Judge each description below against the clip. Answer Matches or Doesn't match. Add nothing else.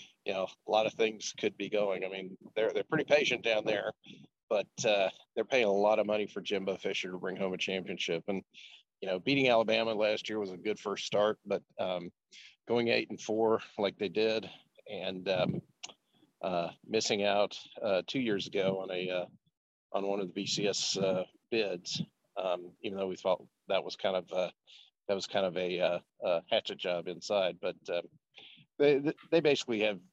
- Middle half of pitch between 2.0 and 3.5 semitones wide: Matches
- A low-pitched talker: Matches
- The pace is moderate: Matches